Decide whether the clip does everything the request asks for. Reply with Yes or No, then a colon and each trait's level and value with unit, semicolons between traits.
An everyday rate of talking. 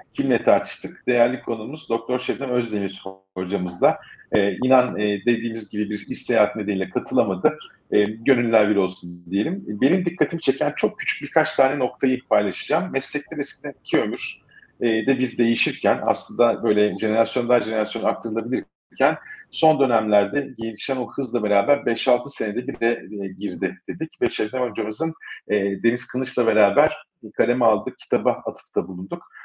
No: fast, 145 wpm